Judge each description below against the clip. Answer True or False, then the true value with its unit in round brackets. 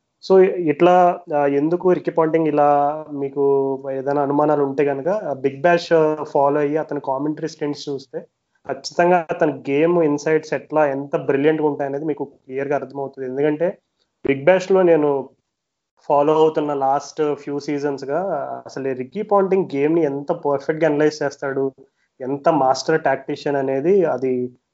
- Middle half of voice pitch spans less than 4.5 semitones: True (2.5 semitones)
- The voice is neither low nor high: True (145 Hz)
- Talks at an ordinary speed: False (135 wpm)